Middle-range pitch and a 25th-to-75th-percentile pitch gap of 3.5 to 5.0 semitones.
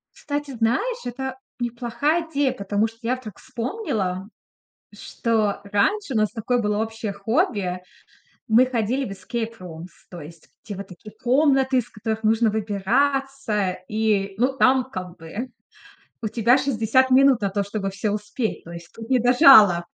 No: high, 225 Hz; average, 4.3 semitones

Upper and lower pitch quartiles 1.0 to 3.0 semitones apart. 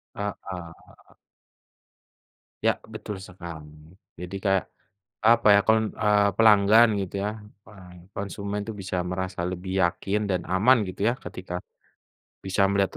Yes: narrow, 2.5 semitones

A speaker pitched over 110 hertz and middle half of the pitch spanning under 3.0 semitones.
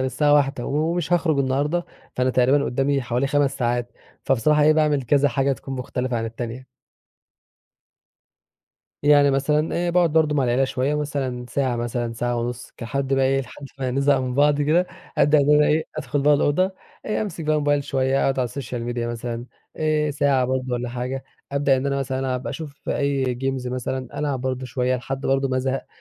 Yes: low, 135 Hz; narrow, 2.5 semitones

